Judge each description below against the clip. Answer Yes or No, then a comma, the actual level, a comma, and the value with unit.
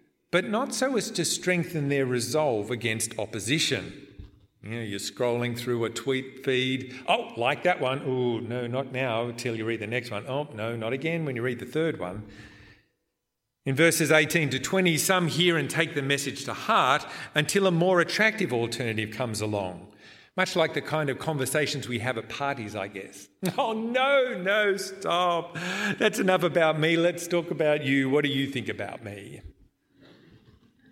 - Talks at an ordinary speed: Yes, average, 180 wpm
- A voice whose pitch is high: No, low, 135 Hz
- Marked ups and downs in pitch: Yes, wide, 6.3 semitones